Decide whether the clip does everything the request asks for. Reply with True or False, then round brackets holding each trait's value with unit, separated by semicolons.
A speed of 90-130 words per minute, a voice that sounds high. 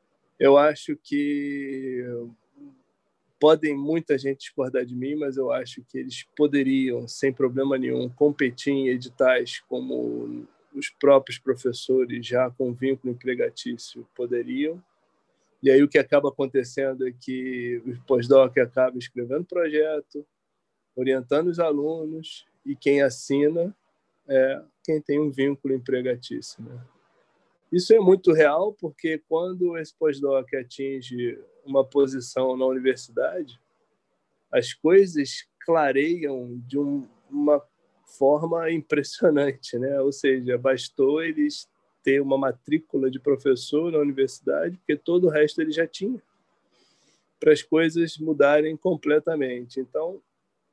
False (120 wpm; 140 Hz)